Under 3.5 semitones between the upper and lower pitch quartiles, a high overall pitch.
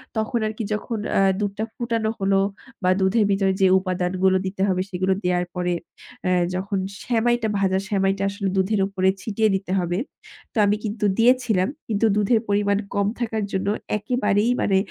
Yes: narrow, 2.5 semitones; high, 200 Hz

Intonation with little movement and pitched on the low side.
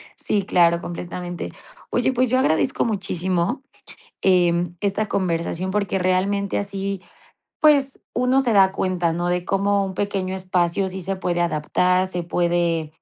No: narrow, 2.3 semitones; medium, 185 Hz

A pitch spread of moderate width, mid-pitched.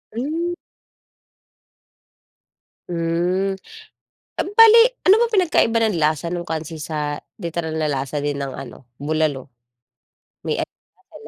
No: wide, 7.1 semitones; medium, 165 Hz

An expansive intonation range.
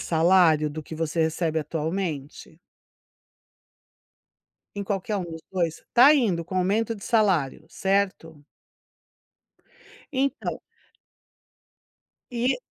No: average, 4.1 semitones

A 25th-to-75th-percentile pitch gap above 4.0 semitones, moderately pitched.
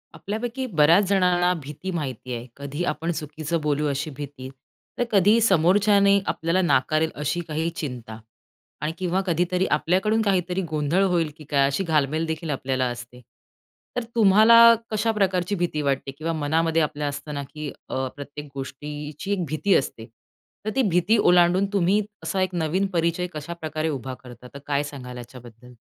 Yes: average, 4.5 semitones; medium, 160 Hz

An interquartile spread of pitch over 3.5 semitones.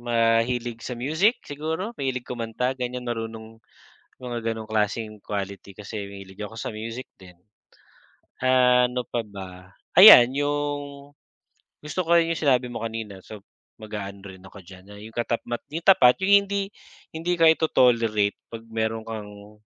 Yes: average, 4.0 semitones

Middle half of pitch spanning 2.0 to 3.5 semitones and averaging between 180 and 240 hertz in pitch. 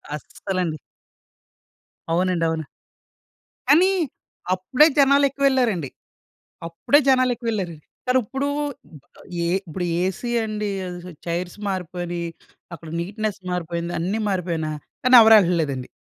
No: wide, 5.8 semitones; medium, 185 Hz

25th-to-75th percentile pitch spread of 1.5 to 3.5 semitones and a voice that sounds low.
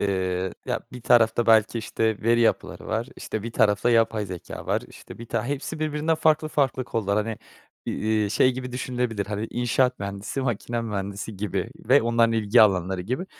Yes: average, 3.2 semitones; low, 115 Hz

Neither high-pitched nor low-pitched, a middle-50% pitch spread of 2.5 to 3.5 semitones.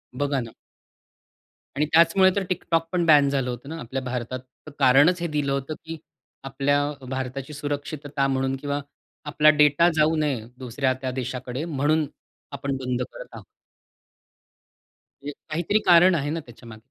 Yes: medium, 145 Hz; average, 2.9 semitones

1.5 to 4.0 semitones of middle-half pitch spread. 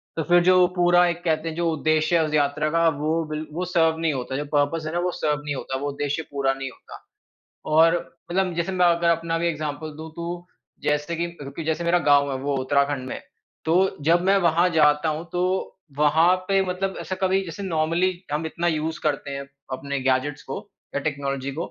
Yes: average, 3.0 semitones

